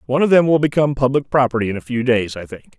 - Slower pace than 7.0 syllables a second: No, 7.2 syllables/s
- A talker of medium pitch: No, low, 130 Hz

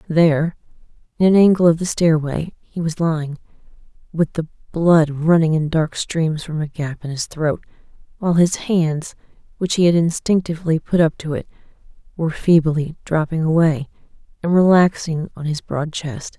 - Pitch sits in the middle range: Yes, medium, 160 Hz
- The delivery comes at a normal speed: Yes, average, 160 wpm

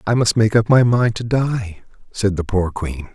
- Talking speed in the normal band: No, fast, 230 wpm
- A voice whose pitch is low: Yes, low, 105 Hz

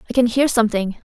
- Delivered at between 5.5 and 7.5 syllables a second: Yes, 7.2 syllables/s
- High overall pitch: Yes, high, 230 Hz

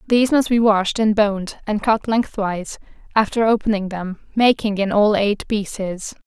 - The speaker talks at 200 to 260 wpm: No, average, 165 wpm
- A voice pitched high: Yes, high, 210 Hz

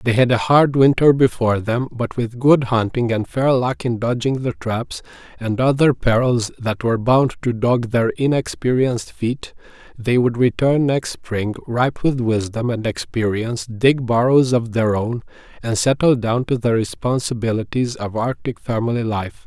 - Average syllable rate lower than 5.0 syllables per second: Yes, 4.6 syllables/s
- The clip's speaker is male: Yes, male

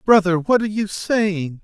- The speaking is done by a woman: No, male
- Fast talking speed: No, average, 185 wpm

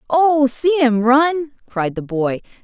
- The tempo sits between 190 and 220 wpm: No, average, 160 wpm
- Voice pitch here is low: No, very high, 260 Hz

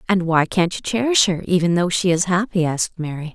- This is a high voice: No, medium, 180 Hz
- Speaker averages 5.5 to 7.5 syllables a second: Yes, 5.7 syllables/s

